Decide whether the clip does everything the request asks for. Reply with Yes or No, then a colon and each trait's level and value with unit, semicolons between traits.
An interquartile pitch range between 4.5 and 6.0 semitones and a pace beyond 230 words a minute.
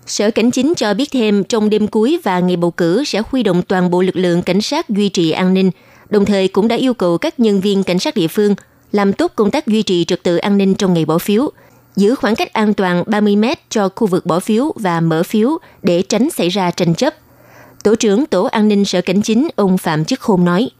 No: average, 3.7 semitones; fast, 250 wpm